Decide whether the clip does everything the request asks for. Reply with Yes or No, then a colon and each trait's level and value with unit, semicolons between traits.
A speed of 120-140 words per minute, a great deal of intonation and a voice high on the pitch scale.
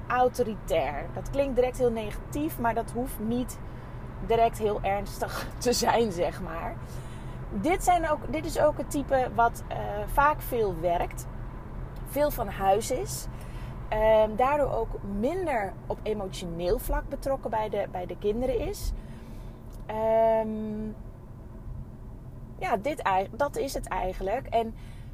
Yes: slow, 135 wpm; wide, 5.7 semitones; high, 225 Hz